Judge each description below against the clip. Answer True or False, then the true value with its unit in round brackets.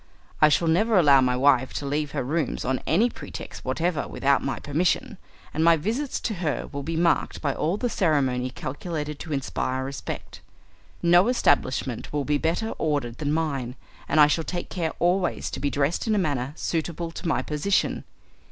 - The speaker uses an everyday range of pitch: True (3.8 semitones)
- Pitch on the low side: False (155 Hz)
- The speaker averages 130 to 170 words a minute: False (185 wpm)